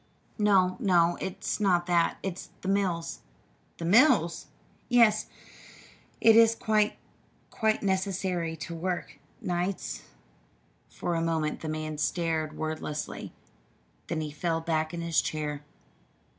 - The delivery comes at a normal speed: No, slow, 120 wpm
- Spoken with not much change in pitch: No, average, 3.3 semitones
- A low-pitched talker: No, medium, 175 Hz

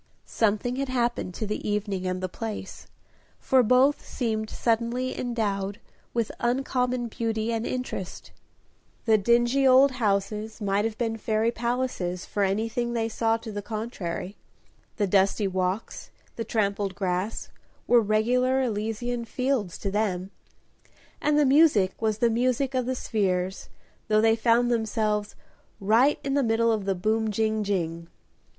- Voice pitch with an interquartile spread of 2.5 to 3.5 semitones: Yes, average, 3.0 semitones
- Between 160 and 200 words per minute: No, average, 145 wpm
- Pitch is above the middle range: Yes, high, 225 Hz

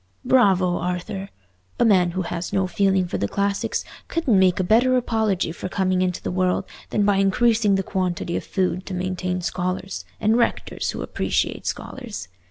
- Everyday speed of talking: Yes, average, 170 wpm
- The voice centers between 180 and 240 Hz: Yes, high, 190 Hz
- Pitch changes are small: Yes, narrow, 2.1 semitones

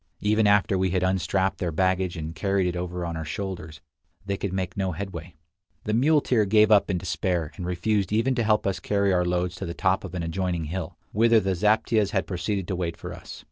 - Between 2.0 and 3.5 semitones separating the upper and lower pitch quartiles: Yes, narrow, 2.6 semitones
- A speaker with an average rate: No, fast, 220 wpm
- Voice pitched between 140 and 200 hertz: No, very low, 95 Hz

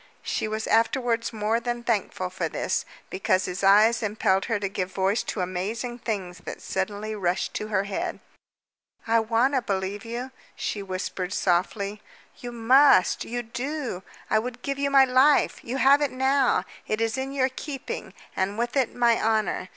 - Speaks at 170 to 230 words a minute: Yes, average, 175 wpm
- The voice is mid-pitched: No, high, 225 Hz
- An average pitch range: Yes, average, 4.1 semitones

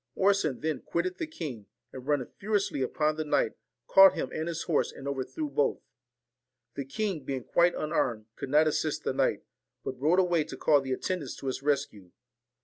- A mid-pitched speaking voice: Yes, medium, 150 Hz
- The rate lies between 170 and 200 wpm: Yes, average, 185 wpm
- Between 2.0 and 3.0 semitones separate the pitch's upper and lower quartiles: No, average, 4.5 semitones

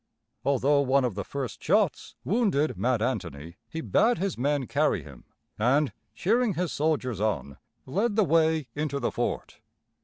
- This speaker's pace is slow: No, average, 155 wpm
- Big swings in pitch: Yes, wide, 5.7 semitones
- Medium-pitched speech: Yes, medium, 145 Hz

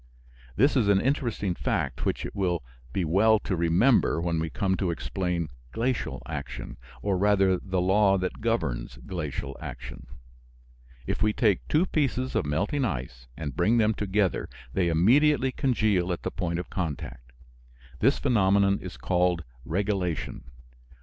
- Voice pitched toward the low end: Yes, very low, 95 Hz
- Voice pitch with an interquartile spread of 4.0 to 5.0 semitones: Yes, average, 4.4 semitones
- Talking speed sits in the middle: Yes, average, 150 wpm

